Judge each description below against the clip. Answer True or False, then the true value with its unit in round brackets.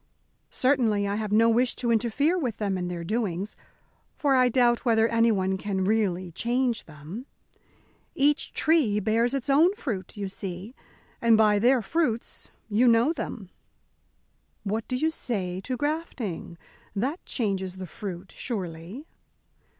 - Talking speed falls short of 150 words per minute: True (140 wpm)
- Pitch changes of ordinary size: True (4.7 semitones)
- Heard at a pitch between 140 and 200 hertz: False (225 Hz)